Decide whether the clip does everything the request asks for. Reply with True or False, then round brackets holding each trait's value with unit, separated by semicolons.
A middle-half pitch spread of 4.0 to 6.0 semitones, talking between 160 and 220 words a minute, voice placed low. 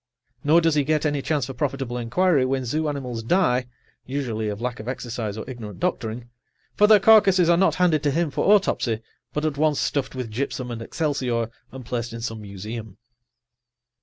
True (4.9 semitones; 190 wpm; 130 Hz)